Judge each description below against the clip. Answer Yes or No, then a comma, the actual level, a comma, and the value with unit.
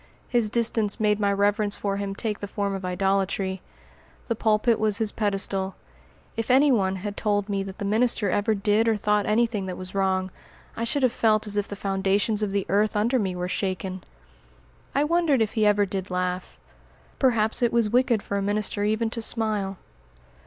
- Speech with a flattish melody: Yes, narrow, 2.2 semitones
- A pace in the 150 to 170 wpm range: No, average, 195 wpm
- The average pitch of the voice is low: No, high, 205 Hz